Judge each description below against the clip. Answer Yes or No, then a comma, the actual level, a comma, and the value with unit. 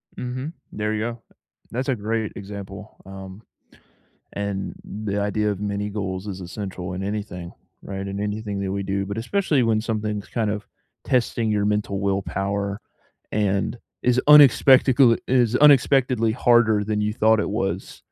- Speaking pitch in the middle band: No, low, 105 Hz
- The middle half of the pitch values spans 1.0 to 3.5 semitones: Yes, narrow, 2.6 semitones